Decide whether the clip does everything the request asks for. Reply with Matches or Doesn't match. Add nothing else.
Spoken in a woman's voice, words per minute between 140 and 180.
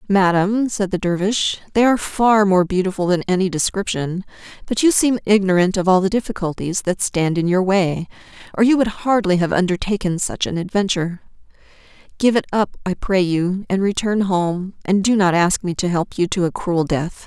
Doesn't match